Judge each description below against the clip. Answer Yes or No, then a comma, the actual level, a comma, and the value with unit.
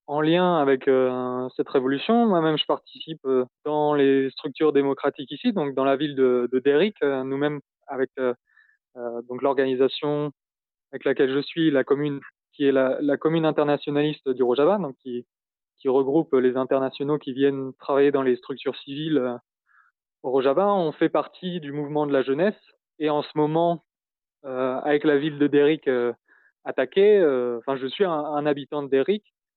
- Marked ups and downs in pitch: No, narrow, 2.4 semitones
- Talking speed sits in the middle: Yes, average, 175 wpm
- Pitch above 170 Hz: No, medium, 140 Hz